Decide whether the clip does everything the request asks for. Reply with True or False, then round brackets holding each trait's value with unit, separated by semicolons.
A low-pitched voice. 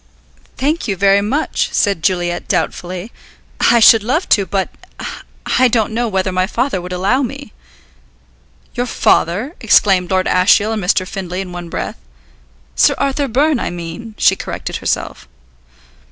False (200 Hz)